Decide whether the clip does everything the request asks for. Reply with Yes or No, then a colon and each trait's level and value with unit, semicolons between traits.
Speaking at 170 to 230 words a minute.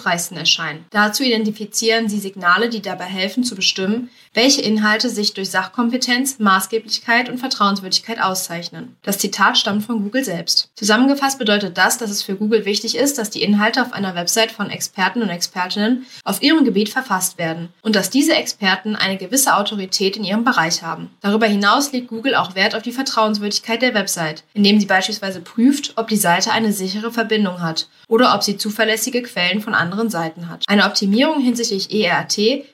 Yes: average, 175 wpm